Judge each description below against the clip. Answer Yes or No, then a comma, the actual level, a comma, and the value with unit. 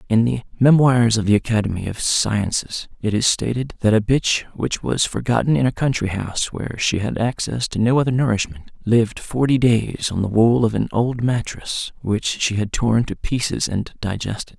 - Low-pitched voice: Yes, low, 115 Hz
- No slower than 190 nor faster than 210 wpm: Yes, average, 195 wpm